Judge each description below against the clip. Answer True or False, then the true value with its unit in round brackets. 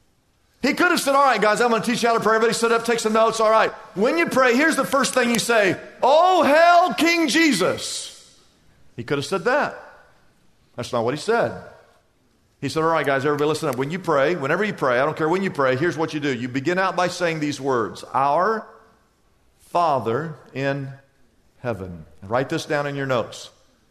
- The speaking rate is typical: False (220 wpm)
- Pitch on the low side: False (185 Hz)